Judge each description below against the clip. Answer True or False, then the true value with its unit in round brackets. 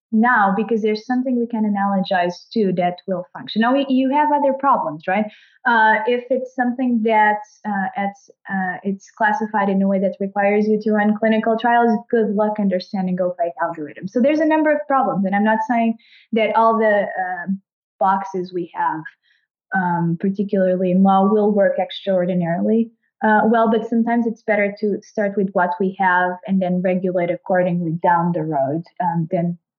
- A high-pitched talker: True (205 Hz)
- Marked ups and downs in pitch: False (3.6 semitones)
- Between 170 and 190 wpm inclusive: True (180 wpm)